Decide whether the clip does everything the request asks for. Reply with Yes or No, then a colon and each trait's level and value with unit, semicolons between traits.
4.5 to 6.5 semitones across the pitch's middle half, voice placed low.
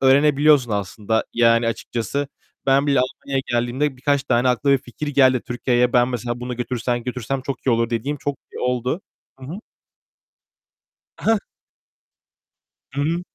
No: narrow, 2.6 semitones; low, 125 Hz